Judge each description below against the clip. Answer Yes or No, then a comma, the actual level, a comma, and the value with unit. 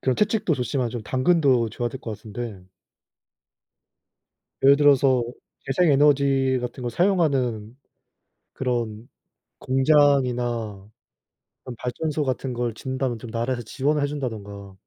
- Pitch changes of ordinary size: Yes, average, 3.0 semitones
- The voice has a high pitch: No, low, 130 Hz